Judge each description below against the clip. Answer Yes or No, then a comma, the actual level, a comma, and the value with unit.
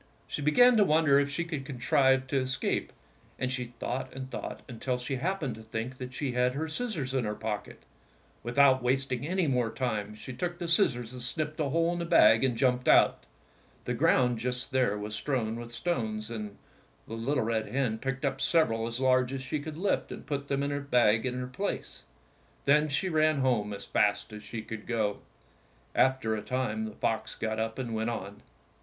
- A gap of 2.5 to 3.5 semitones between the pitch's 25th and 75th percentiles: No, average, 3.9 semitones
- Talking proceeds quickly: Yes, fast, 210 wpm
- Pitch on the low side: Yes, low, 130 Hz